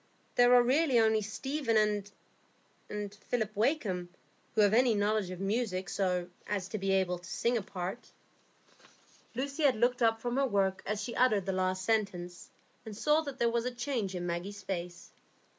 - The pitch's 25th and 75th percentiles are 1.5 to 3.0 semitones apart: No, average, 4.2 semitones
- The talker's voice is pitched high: Yes, high, 215 Hz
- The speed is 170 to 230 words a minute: Yes, average, 175 wpm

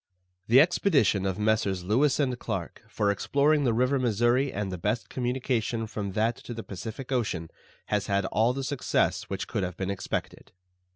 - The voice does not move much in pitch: No, average, 4.3 semitones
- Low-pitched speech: Yes, low, 115 Hz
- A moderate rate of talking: Yes, average, 175 wpm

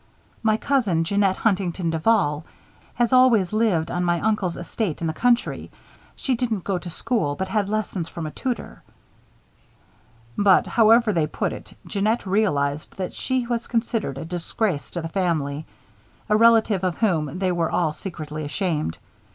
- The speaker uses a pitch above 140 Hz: Yes, high, 190 Hz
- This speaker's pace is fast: No, average, 160 wpm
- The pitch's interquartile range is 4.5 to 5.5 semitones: Yes, average, 5.2 semitones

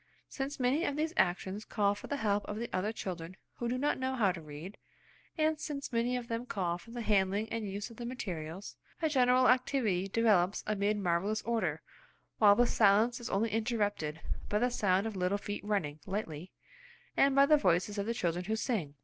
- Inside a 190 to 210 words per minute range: Yes, average, 200 wpm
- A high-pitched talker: Yes, high, 210 Hz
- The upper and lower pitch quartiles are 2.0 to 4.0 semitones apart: No, average, 4.4 semitones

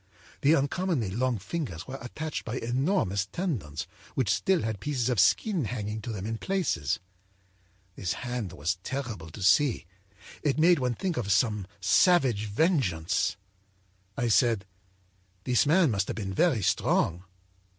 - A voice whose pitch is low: Yes, low, 120 Hz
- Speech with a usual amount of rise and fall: No, wide, 7.0 semitones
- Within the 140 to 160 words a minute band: Yes, average, 145 wpm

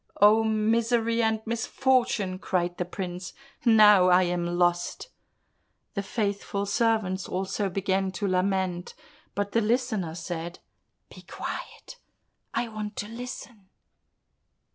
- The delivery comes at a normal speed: No, slow, 115 wpm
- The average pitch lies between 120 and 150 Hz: No, high, 200 Hz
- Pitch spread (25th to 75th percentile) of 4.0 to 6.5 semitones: No, average, 3.4 semitones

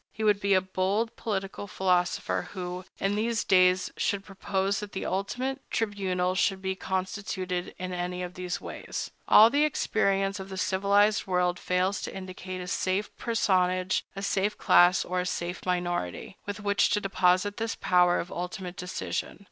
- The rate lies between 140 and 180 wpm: Yes, average, 165 wpm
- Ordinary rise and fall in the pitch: No, narrow, 1.8 semitones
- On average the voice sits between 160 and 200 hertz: Yes, high, 190 Hz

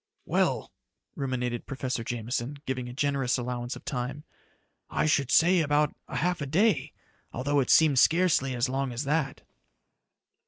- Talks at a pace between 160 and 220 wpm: No, average, 150 wpm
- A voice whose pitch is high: No, low, 135 Hz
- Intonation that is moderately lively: Yes, average, 3.0 semitones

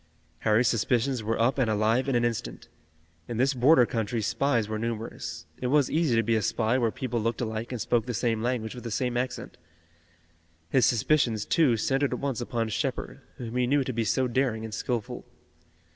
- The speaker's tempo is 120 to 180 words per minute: No, average, 200 wpm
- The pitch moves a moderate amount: No, narrow, 2.3 semitones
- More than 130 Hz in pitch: No, low, 120 Hz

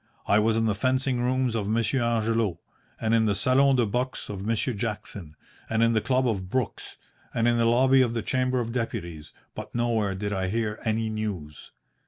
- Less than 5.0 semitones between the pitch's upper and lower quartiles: Yes, average, 2.7 semitones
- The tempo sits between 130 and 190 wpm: No, average, 200 wpm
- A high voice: No, low, 115 Hz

